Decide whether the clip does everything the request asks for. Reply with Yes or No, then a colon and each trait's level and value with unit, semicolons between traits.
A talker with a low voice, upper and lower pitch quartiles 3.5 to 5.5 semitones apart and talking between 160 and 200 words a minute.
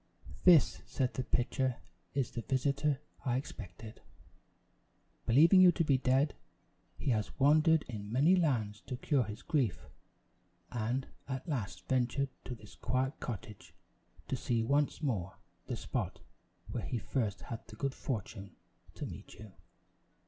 No: low, 130 Hz; average, 4.2 semitones; average, 140 wpm